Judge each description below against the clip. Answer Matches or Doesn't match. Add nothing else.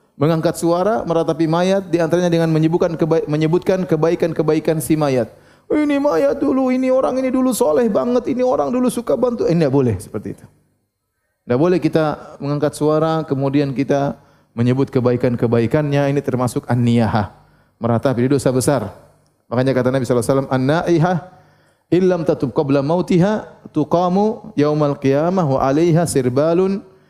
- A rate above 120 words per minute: Matches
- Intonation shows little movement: Doesn't match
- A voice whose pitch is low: Doesn't match